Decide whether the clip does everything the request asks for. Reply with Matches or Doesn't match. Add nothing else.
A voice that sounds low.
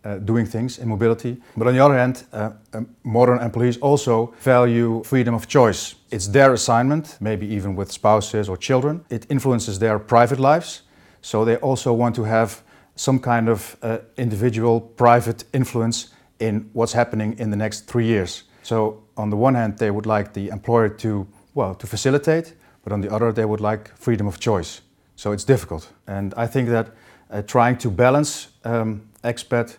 Matches